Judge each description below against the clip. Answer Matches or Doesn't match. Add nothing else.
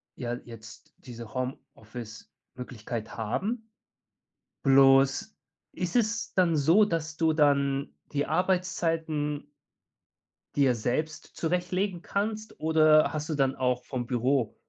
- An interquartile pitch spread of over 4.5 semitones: Matches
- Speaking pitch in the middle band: Matches